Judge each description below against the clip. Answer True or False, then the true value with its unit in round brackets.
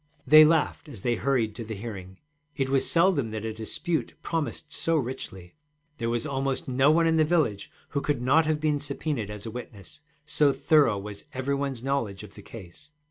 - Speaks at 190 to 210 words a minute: True (195 wpm)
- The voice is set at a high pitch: False (135 Hz)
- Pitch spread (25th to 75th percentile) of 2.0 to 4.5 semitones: False (5.5 semitones)